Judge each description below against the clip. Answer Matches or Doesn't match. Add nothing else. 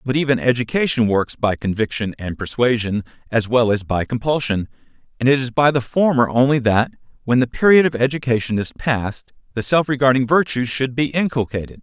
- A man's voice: Matches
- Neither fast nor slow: Matches